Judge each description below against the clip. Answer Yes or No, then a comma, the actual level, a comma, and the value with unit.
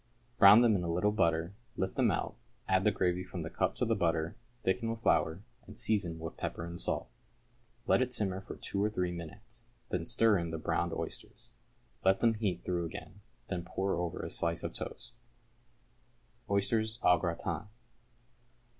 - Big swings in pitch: No, average, 3.9 semitones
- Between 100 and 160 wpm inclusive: No, average, 180 wpm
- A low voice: Yes, very low, 95 Hz